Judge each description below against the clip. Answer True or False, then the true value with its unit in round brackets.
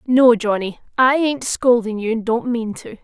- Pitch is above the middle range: True (240 Hz)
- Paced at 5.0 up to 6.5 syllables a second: False (4.5 syllables/s)